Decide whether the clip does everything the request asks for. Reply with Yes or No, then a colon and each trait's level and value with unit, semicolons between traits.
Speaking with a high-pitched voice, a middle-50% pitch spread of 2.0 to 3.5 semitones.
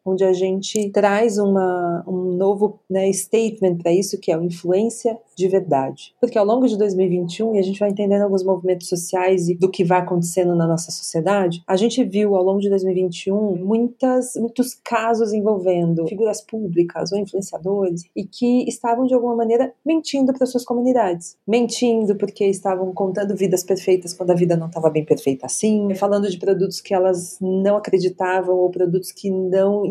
Yes: high, 195 Hz; average, 2.8 semitones